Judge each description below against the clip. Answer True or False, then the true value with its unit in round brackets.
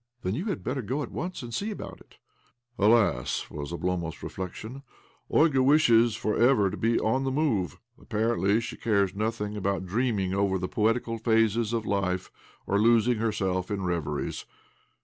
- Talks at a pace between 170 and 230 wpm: True (175 wpm)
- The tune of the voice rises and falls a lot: False (3.9 semitones)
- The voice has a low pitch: True (110 Hz)